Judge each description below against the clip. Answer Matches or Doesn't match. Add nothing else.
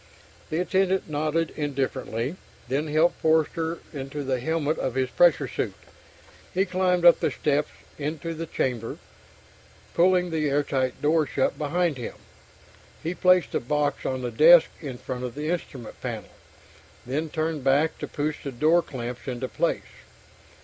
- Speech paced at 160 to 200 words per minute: Doesn't match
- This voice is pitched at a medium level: Matches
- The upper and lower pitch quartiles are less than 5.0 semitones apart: Matches